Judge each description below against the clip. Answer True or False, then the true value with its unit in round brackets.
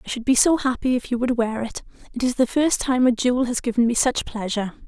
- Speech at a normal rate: False (260 wpm)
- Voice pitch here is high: True (245 Hz)